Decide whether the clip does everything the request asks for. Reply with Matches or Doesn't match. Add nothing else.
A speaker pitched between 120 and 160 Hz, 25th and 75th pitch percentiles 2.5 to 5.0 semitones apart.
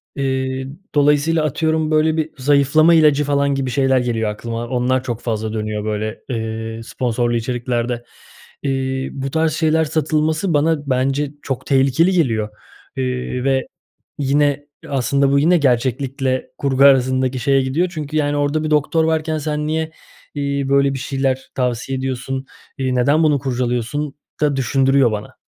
Matches